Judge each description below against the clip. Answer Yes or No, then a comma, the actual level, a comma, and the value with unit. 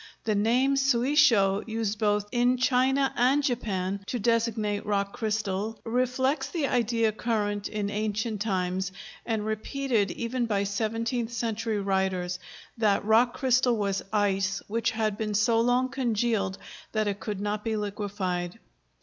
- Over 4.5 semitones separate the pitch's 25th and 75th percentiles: No, average, 3.0 semitones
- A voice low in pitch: No, high, 220 Hz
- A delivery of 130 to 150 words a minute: Yes, average, 140 wpm